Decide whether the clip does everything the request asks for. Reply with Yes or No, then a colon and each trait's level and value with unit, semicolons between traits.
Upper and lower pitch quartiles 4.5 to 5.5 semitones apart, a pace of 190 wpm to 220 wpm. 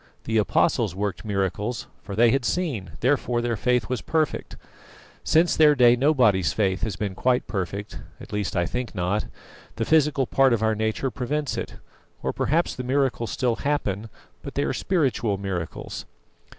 No: average, 4.8 semitones; average, 165 wpm